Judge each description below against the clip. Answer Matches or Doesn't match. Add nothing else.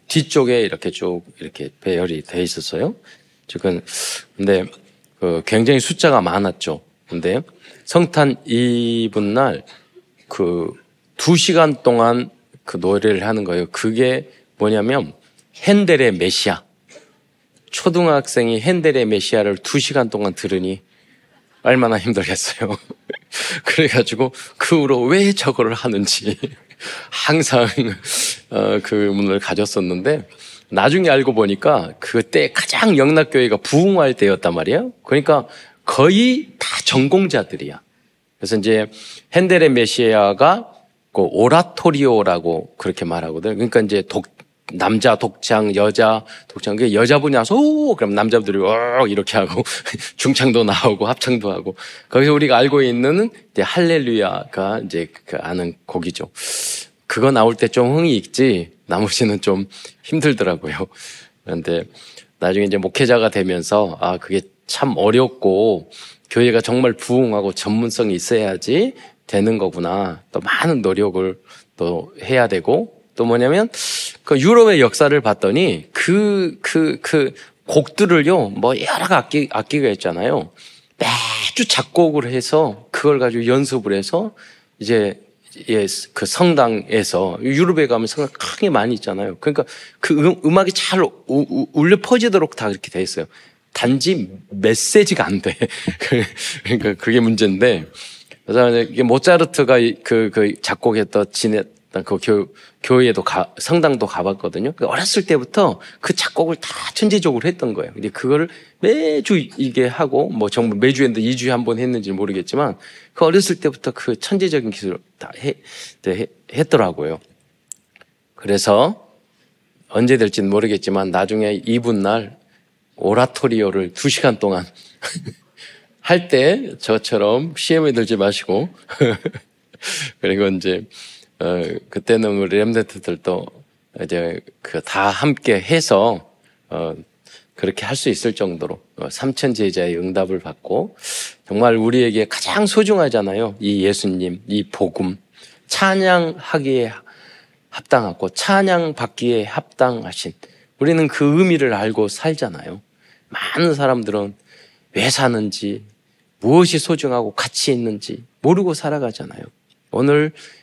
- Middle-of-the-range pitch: Doesn't match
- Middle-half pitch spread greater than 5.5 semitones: Matches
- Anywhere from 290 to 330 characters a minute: Doesn't match